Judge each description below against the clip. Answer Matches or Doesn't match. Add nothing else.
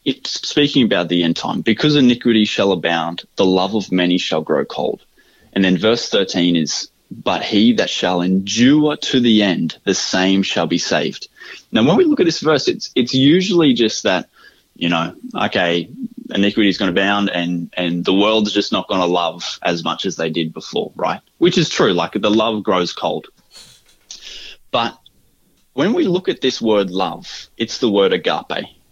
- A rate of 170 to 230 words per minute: Matches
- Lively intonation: Matches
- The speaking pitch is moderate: Doesn't match